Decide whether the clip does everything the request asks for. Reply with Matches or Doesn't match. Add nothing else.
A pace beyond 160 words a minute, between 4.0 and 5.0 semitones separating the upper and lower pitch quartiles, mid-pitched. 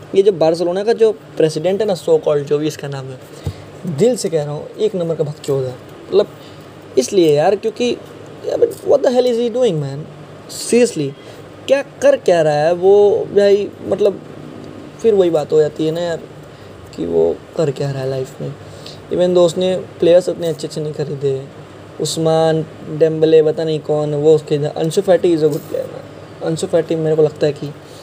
Matches